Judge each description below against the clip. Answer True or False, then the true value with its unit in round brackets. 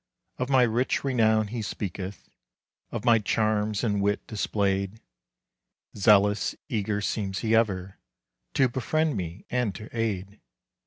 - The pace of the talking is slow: True (125 wpm)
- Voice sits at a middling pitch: False (105 Hz)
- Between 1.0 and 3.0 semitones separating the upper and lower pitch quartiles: True (2.6 semitones)